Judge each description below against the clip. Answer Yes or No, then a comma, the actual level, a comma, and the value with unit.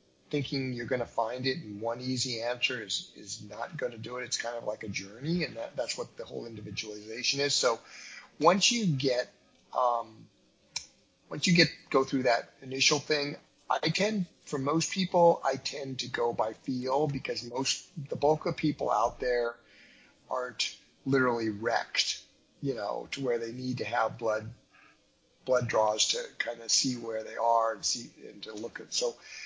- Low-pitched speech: Yes, low, 130 Hz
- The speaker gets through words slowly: No, average, 185 wpm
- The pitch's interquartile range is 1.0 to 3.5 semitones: No, average, 4.2 semitones